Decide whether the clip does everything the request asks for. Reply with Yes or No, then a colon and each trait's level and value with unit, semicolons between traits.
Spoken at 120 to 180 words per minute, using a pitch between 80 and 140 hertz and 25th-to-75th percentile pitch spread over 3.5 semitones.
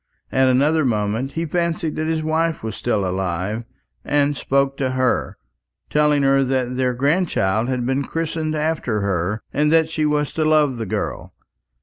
Yes: average, 165 wpm; low, 135 Hz; average, 4.5 semitones